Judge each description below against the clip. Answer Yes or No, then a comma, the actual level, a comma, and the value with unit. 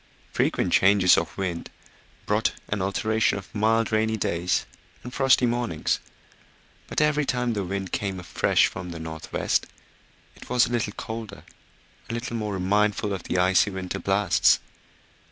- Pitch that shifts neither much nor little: Yes, average, 3.4 semitones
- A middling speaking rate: Yes, average, 155 wpm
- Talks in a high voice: No, low, 105 Hz